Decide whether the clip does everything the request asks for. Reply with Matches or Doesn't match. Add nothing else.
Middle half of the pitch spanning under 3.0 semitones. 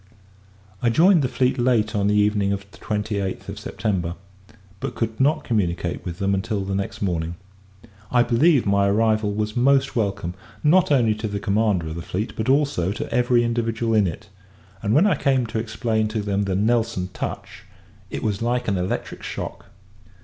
Doesn't match